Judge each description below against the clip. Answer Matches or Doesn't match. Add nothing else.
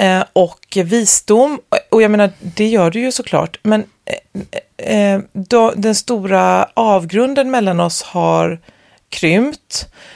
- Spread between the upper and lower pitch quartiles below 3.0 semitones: Doesn't match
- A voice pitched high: Matches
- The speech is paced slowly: Matches